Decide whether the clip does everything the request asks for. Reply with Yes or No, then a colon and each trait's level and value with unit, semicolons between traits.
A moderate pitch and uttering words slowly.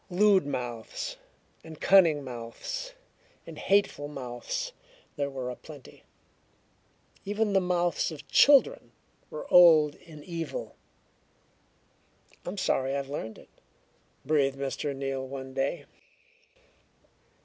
Yes: medium, 150 Hz; slow, 105 wpm